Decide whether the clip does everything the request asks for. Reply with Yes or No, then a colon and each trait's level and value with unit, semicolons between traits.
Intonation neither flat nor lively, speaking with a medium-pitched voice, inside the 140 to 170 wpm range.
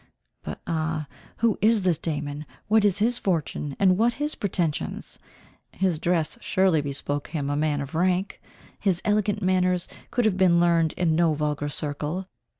Yes: average, 4.2 semitones; medium, 175 Hz; average, 160 wpm